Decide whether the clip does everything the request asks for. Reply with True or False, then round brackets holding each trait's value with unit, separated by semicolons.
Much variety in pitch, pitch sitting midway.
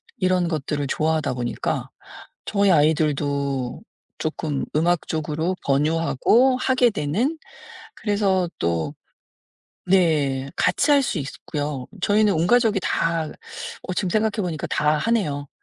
True (5.7 semitones; 160 Hz)